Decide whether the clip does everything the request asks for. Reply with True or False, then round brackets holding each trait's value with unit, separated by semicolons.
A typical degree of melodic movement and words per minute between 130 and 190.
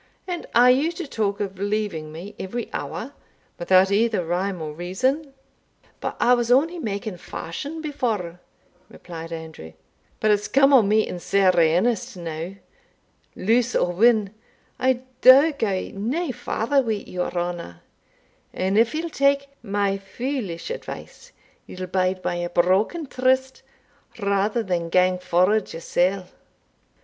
False (5.7 semitones; 140 wpm)